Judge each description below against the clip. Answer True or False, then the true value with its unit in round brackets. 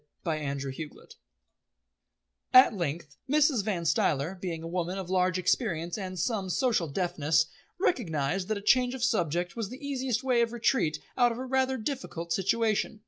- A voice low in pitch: False (190 Hz)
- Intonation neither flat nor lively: False (6.5 semitones)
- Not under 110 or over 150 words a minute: False (160 wpm)